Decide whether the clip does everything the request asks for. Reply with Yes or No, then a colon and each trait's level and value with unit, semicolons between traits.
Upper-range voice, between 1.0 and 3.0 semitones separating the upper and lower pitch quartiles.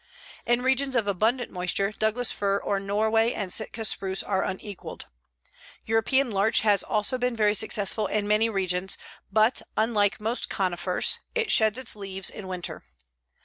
Yes: high, 210 Hz; narrow, 2.5 semitones